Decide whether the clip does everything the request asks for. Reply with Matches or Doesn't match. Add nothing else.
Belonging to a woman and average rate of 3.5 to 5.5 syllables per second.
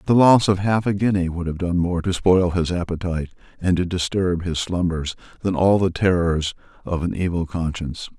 Doesn't match